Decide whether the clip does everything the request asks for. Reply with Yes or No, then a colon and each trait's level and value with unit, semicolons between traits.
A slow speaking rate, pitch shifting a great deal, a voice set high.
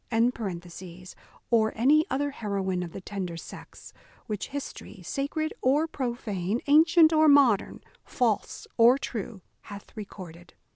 Yes: slow, 125 wpm; wide, 6.3 semitones; high, 235 Hz